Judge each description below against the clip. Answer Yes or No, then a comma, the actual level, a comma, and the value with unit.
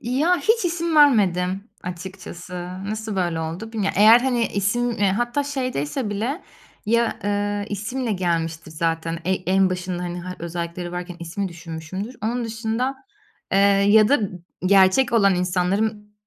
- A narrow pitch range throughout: No, average, 4.6 semitones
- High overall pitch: Yes, high, 200 Hz